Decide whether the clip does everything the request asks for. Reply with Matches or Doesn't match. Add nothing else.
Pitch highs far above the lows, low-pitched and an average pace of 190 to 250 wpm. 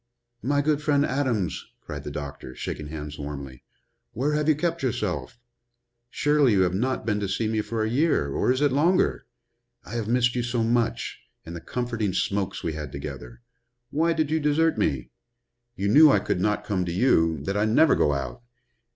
Matches